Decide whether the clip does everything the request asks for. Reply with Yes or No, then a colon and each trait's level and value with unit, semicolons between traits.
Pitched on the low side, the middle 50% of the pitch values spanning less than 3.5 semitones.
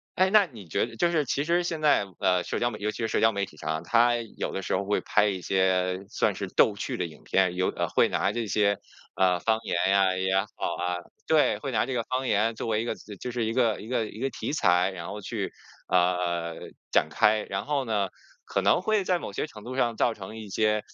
No: low, 105 Hz; average, 4.4 semitones